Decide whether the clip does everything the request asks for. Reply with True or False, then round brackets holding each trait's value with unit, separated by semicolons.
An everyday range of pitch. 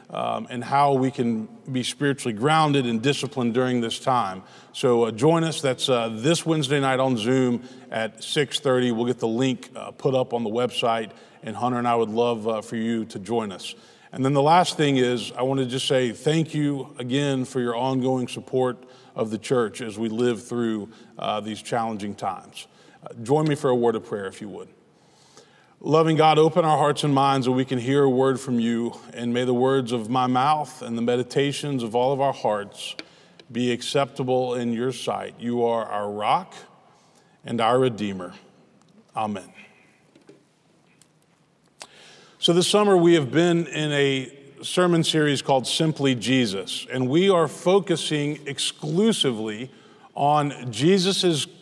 True (3.5 semitones)